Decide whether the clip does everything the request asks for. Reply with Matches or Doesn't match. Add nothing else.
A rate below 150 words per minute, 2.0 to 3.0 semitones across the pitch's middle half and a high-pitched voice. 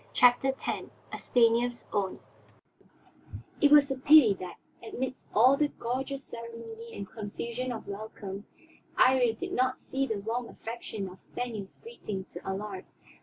Doesn't match